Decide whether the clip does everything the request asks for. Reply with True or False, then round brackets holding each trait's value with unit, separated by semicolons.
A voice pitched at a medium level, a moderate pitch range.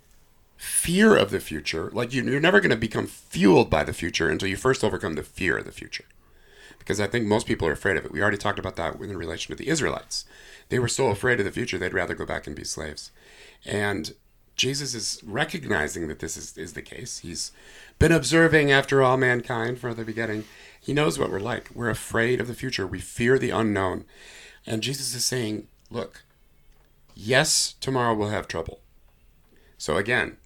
False (115 Hz; 3.9 semitones)